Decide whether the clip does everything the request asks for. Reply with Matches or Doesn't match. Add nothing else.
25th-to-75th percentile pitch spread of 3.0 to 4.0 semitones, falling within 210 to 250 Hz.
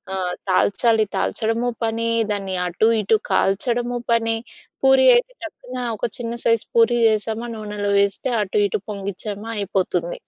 Doesn't match